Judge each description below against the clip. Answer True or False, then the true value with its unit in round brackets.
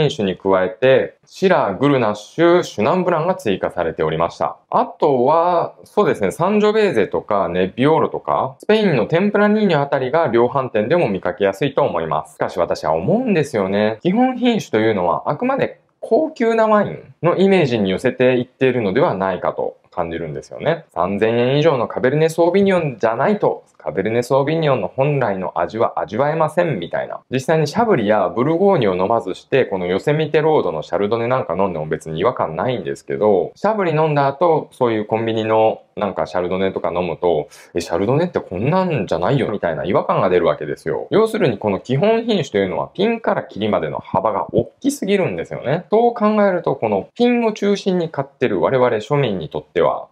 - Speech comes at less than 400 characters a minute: False (445 characters per minute)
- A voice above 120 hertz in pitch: True (140 Hz)